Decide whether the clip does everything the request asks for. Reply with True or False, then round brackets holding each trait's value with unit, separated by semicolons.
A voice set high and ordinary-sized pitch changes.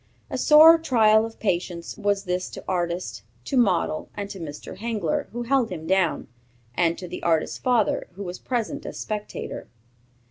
True (200 Hz; 4.8 semitones)